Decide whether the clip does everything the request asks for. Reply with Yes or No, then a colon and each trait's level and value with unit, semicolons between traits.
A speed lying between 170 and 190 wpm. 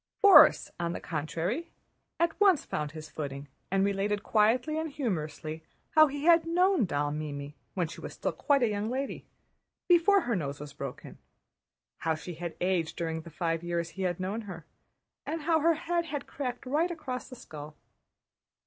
Yes: average, 180 wpm